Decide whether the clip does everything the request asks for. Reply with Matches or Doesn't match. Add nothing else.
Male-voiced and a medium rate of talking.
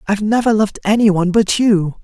Matches